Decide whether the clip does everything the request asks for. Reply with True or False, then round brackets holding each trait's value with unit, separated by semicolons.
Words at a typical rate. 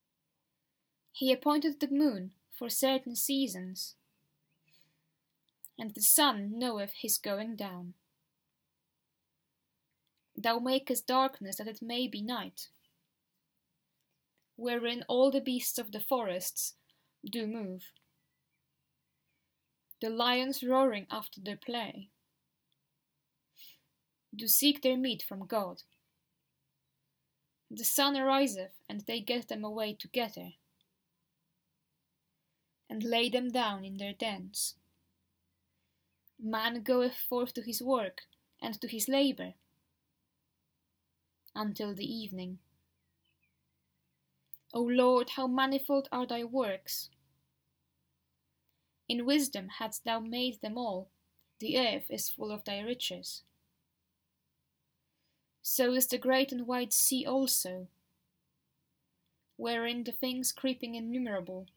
False (105 wpm)